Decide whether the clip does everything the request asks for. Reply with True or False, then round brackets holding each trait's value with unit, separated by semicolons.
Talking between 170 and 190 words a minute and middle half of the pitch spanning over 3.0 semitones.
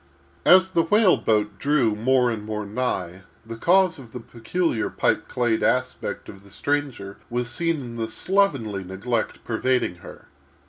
False (155 wpm; 5.3 semitones)